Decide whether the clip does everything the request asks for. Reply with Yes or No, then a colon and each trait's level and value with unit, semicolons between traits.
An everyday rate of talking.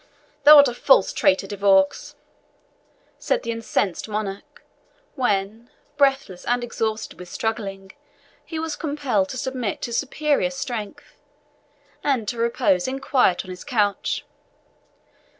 No: slow, 130 wpm